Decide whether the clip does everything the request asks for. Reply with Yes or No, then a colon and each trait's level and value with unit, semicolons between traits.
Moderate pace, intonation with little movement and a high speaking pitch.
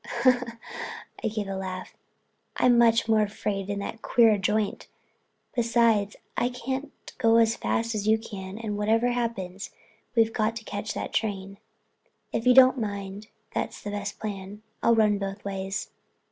Yes: average, 155 wpm; narrow, 2.3 semitones; high, 215 Hz